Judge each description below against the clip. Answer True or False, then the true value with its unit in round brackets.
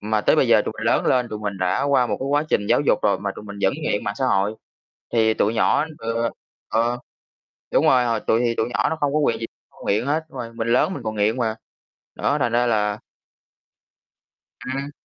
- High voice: False (115 Hz)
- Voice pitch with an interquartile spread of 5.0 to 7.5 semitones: False (3.4 semitones)